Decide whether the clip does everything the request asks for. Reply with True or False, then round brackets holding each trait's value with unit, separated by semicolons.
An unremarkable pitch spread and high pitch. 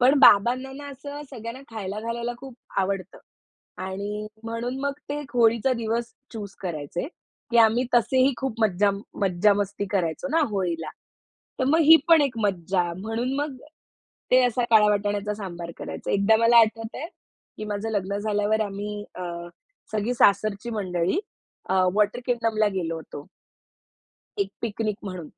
True (3.4 semitones; 215 Hz)